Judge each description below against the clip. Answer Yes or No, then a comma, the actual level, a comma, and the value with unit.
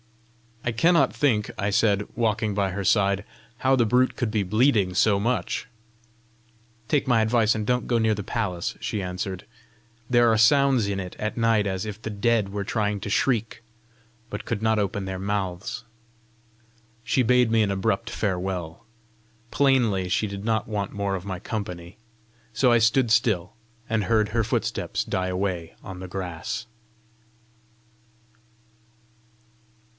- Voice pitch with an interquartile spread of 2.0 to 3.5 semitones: Yes, average, 3.0 semitones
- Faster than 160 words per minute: No, average, 155 wpm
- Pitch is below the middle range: Yes, low, 105 Hz